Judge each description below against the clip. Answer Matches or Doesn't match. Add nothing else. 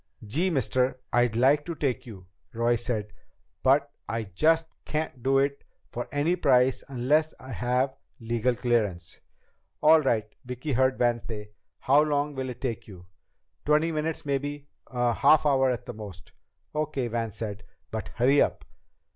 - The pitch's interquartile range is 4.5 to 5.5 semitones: Doesn't match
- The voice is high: Doesn't match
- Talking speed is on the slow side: Doesn't match